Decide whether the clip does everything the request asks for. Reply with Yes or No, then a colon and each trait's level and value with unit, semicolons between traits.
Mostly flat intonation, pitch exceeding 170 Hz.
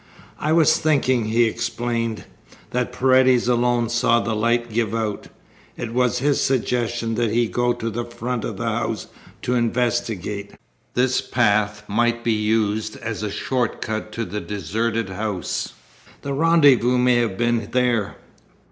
No: narrow, 2.1 semitones; low, 120 Hz